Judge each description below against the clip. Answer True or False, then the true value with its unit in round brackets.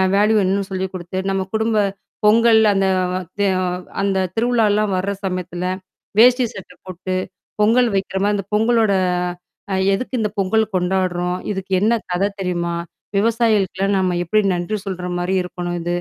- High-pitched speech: True (195 Hz)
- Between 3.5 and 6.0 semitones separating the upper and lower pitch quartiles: False (3.0 semitones)